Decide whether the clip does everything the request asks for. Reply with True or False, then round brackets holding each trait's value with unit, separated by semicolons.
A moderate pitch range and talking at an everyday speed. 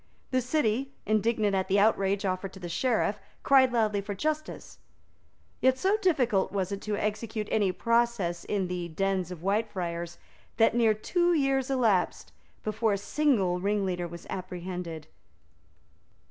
True (4.3 semitones; 145 wpm)